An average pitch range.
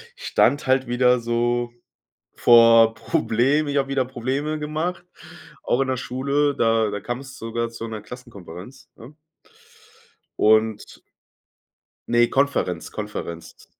Yes: average, 3.3 semitones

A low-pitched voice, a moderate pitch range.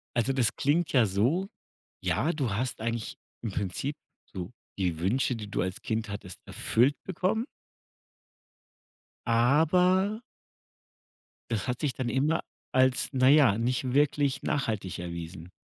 No: low, 125 Hz; wide, 5.9 semitones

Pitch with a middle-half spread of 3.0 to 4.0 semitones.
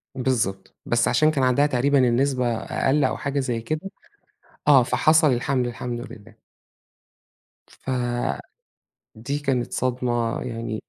No: narrow, 2.5 semitones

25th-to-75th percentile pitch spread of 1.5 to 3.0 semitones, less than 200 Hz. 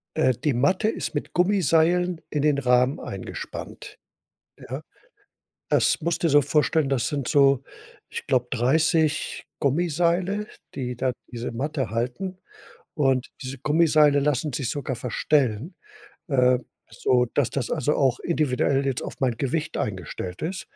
No: average, 4.0 semitones; medium, 140 Hz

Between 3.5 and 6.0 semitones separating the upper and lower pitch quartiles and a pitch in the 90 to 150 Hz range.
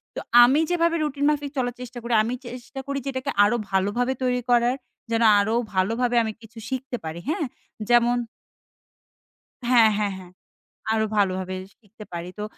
No: average, 3.8 semitones; high, 240 Hz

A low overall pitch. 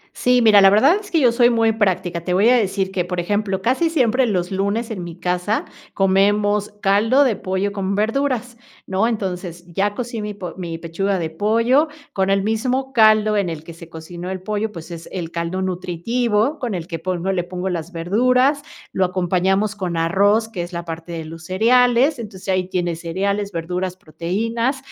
No: high, 195 Hz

